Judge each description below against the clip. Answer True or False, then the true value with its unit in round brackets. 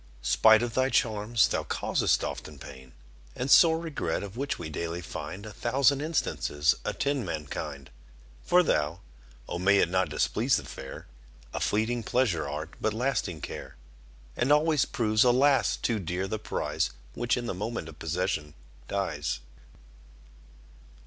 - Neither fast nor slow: True (150 wpm)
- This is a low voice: True (105 Hz)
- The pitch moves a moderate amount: False (7.3 semitones)